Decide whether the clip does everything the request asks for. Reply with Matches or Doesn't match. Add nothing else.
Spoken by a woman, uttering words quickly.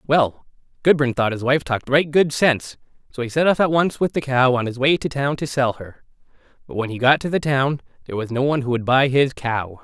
Doesn't match